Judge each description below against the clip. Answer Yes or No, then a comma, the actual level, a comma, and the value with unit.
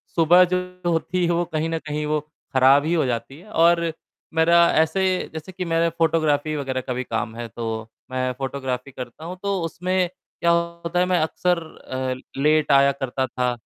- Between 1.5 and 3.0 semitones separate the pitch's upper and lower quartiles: No, average, 4.1 semitones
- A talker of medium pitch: Yes, medium, 155 Hz